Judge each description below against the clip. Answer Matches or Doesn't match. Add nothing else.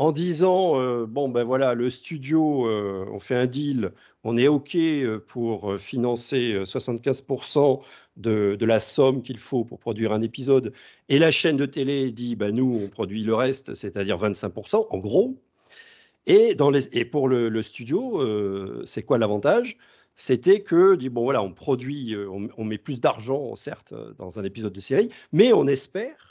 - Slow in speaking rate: Doesn't match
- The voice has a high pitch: Doesn't match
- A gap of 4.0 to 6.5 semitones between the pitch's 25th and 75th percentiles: Matches